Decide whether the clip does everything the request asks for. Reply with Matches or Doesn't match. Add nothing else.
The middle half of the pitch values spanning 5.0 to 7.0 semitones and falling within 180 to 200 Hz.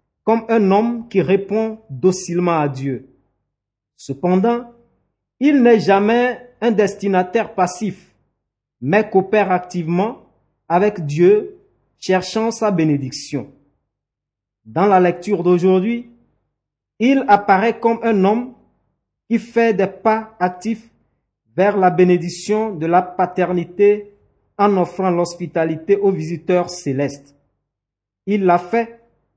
Matches